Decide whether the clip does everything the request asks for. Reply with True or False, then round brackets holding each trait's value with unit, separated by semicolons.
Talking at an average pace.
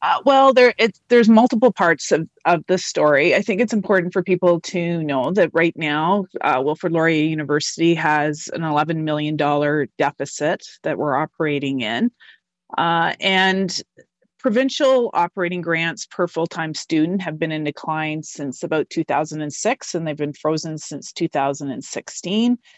True (150 wpm)